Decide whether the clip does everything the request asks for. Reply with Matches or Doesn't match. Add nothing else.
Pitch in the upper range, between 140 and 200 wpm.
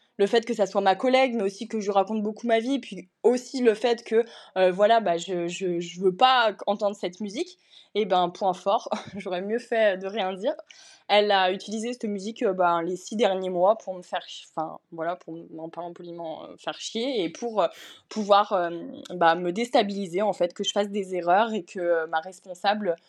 Doesn't match